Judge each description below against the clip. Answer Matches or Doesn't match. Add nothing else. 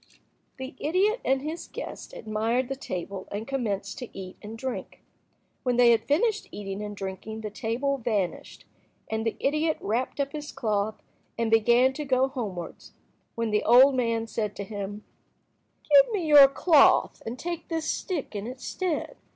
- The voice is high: Matches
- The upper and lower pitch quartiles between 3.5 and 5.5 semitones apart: Matches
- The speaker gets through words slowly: Doesn't match